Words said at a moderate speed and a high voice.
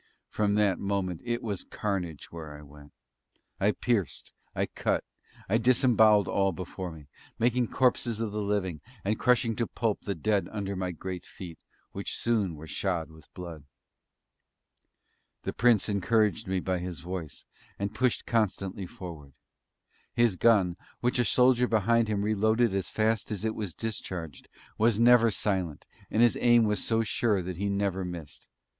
No: average, 160 wpm; low, 100 Hz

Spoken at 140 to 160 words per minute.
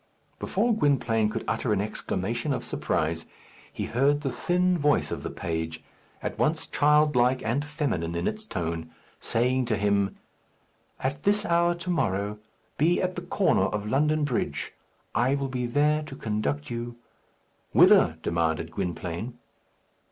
Yes: average, 150 wpm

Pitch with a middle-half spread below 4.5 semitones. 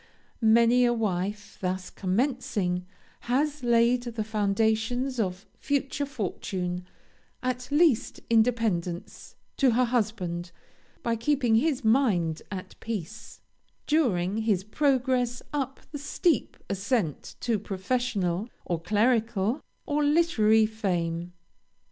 No: average, 4.8 semitones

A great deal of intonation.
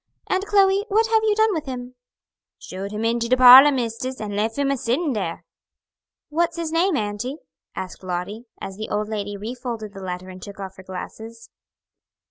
Yes: wide, 6.3 semitones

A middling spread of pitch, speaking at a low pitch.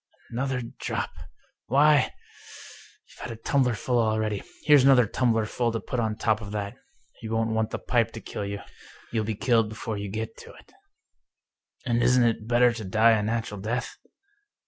No: narrow, 2.3 semitones; low, 115 Hz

